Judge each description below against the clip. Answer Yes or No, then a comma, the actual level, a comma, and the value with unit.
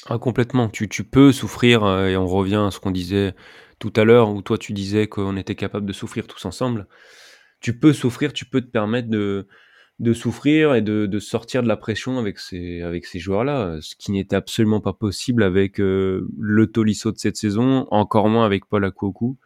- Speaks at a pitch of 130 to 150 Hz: No, low, 105 Hz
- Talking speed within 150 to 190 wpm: No, average, 205 wpm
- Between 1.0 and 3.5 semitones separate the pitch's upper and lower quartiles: Yes, average, 3.1 semitones